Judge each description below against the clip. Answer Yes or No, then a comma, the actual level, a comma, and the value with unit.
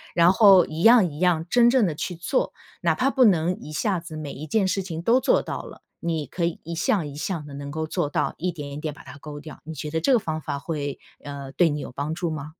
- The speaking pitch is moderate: Yes, medium, 160 Hz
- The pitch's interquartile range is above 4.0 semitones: No, average, 3.6 semitones